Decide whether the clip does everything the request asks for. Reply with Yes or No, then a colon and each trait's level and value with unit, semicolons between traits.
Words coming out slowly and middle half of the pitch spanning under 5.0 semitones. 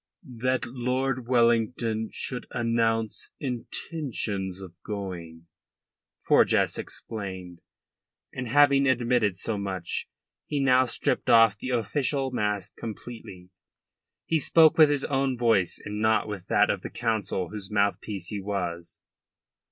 Yes: slow, 120 wpm; average, 4.3 semitones